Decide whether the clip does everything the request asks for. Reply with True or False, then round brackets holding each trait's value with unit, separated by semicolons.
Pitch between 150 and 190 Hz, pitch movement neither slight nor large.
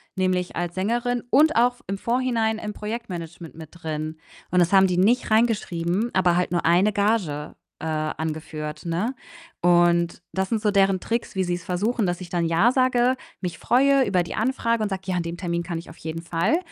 True (185 Hz; 5.0 semitones)